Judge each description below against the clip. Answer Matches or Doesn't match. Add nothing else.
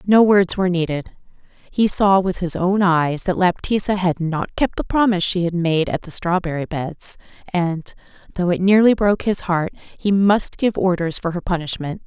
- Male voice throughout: Doesn't match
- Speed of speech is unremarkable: Matches